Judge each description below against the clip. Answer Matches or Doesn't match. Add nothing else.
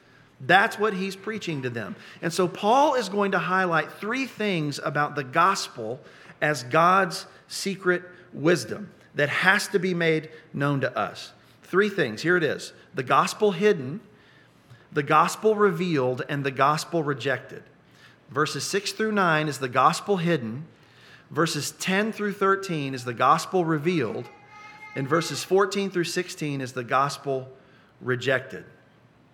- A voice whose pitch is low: Doesn't match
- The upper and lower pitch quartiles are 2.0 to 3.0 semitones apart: Doesn't match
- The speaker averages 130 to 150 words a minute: Matches